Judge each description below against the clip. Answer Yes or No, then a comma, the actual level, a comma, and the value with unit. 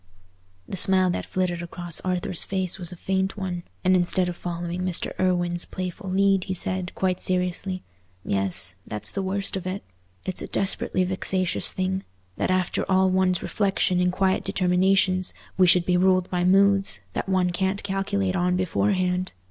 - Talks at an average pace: Yes, average, 165 wpm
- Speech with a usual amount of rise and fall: No, narrow, 1.1 semitones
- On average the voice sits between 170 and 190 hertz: Yes, medium, 185 Hz